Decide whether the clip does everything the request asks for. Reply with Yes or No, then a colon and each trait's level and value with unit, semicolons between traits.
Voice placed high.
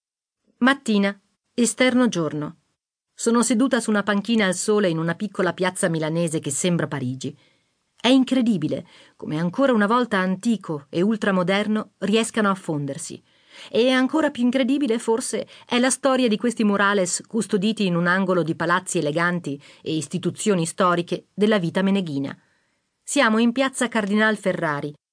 Yes: high, 200 Hz